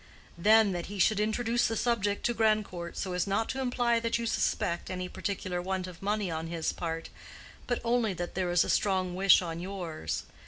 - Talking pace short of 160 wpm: No, average, 200 wpm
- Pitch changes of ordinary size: Yes, average, 3.9 semitones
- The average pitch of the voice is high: Yes, high, 195 Hz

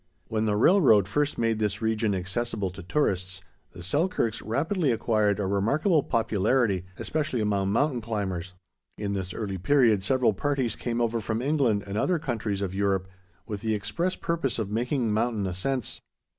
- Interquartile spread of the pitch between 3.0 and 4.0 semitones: No, average, 4.4 semitones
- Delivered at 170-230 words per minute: No, average, 160 wpm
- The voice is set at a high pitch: No, low, 110 Hz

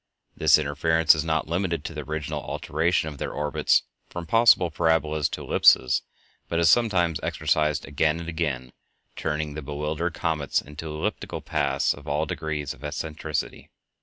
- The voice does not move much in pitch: Yes, narrow, 1.7 semitones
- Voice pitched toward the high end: No, very low, 80 Hz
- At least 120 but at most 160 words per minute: Yes, average, 155 wpm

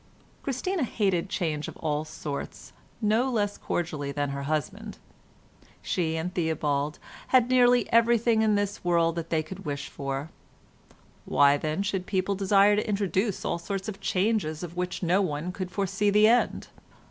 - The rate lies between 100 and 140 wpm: No, average, 160 wpm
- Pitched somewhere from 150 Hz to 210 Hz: Yes, medium, 185 Hz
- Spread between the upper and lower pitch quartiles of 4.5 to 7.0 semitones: Yes, average, 5.0 semitones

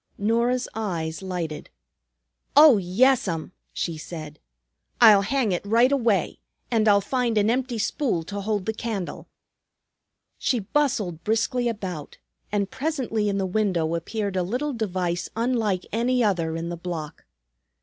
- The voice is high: Yes, high, 205 Hz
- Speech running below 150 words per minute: Yes, average, 140 wpm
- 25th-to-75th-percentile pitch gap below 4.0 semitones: No, average, 4.9 semitones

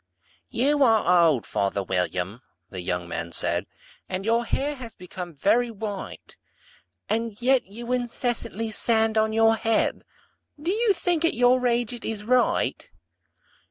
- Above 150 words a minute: No, average, 145 wpm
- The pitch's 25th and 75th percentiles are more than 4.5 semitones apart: Yes, average, 5.1 semitones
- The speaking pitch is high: Yes, high, 225 Hz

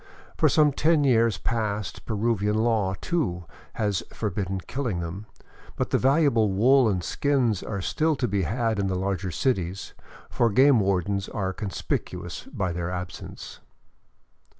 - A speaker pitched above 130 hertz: No, low, 105 Hz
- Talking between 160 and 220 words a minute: No, average, 145 wpm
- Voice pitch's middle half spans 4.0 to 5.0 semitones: Yes, average, 4.4 semitones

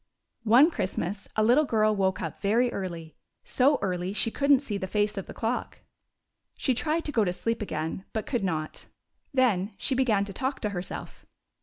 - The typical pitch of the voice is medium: No, high, 215 Hz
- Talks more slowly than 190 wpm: No, average, 195 wpm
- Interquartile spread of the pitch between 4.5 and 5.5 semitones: Yes, average, 5.0 semitones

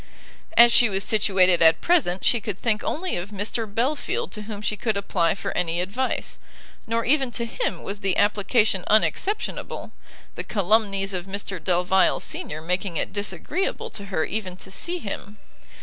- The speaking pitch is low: No, high, 205 Hz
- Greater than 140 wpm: Yes, average, 165 wpm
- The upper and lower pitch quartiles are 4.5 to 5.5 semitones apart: No, average, 3.6 semitones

